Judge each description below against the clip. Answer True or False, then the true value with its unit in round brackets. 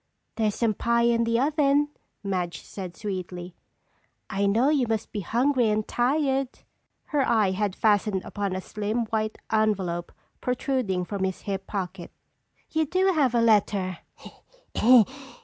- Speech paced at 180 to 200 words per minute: False (140 wpm)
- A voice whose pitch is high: True (215 Hz)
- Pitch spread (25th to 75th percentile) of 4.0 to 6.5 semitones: True (4.3 semitones)